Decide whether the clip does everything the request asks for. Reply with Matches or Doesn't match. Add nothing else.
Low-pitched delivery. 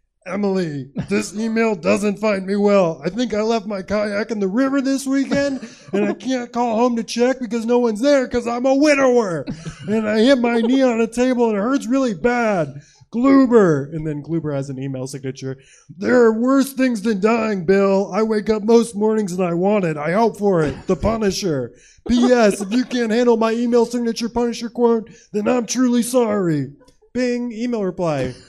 Doesn't match